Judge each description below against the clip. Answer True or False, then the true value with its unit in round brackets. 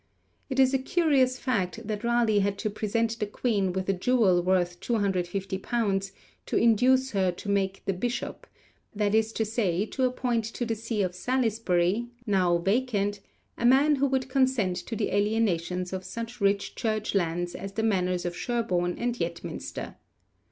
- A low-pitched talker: False (210 Hz)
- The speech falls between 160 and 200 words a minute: True (165 wpm)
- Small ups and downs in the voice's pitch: False (4.1 semitones)